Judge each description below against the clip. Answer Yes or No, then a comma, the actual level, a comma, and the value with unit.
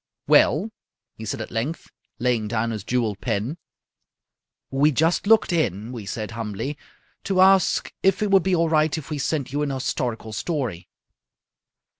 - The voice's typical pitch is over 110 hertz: Yes, low, 135 Hz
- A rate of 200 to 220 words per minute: No, average, 160 wpm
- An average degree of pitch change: No, wide, 6.6 semitones